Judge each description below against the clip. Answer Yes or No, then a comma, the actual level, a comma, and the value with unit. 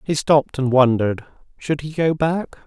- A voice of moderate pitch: Yes, medium, 145 Hz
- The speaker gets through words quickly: No, average, 155 wpm